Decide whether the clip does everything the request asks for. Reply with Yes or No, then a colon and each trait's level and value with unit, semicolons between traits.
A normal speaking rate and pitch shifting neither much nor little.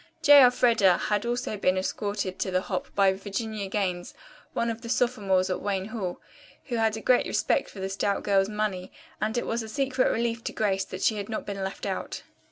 No: fast, 210 wpm; average, 3.1 semitones